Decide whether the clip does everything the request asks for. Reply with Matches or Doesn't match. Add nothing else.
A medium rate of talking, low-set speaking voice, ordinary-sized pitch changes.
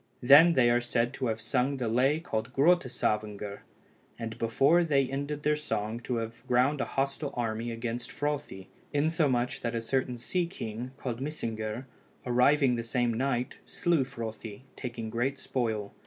Matches